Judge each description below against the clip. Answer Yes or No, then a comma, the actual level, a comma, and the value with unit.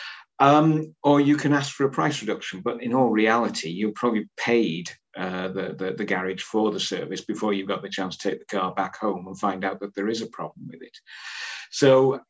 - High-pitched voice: No, low, 105 Hz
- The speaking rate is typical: No, fast, 230 wpm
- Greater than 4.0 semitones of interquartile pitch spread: Yes, wide, 5.6 semitones